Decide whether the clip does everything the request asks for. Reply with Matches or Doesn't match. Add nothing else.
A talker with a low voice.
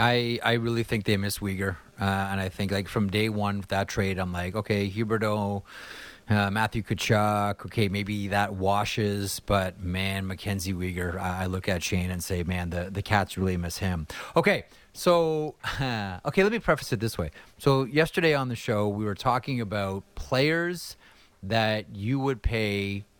Matches